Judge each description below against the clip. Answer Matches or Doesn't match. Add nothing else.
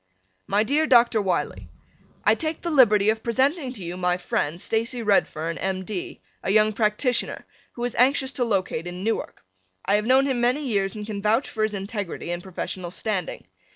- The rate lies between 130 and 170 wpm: Doesn't match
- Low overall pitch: Doesn't match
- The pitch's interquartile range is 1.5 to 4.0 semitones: Doesn't match